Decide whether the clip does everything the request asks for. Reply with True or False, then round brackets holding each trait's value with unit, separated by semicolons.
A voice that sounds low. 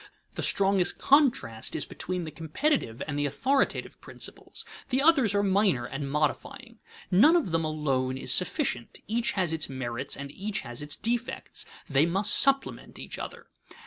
False (180 Hz)